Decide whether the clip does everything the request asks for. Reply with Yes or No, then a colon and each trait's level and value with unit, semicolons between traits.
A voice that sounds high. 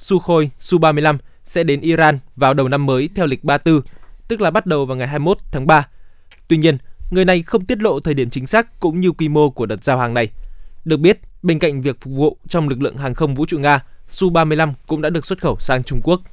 No: medium, 150 Hz